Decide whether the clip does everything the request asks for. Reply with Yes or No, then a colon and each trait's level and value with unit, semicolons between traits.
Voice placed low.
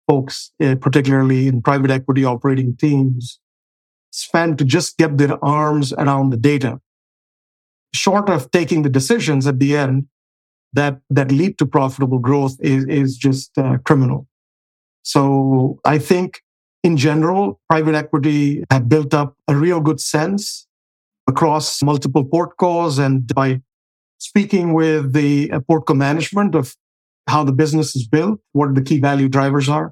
No: medium, 145 Hz